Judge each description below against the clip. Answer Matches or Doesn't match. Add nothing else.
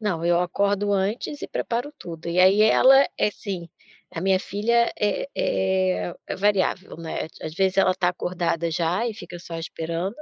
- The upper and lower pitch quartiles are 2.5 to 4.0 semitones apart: Matches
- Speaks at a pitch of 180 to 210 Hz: Matches